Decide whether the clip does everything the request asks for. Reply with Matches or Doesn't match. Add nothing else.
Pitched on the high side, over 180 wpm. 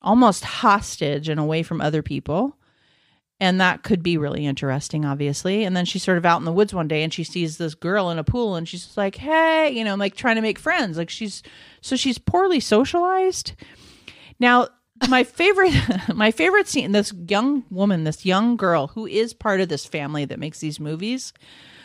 Matches